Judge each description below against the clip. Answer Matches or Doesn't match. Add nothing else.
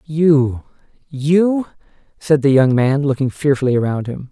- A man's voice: Matches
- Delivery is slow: Matches